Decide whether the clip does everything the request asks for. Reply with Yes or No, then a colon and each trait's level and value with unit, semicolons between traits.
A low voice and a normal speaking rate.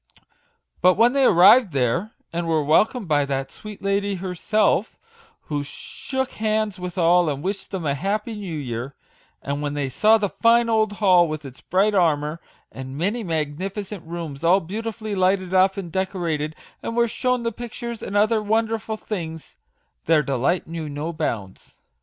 No: medium, 185 Hz; average, 170 wpm